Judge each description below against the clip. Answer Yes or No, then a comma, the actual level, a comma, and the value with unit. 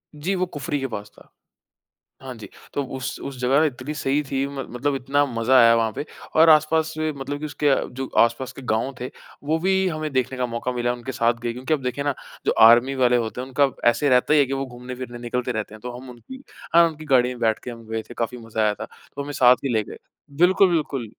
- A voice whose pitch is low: Yes, low, 130 Hz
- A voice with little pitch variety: No, average, 3.3 semitones